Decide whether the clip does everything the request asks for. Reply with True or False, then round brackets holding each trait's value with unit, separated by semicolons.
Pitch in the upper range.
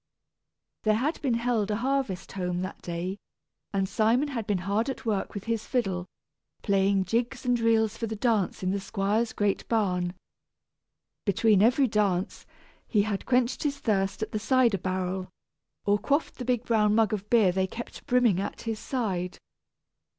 True (215 Hz)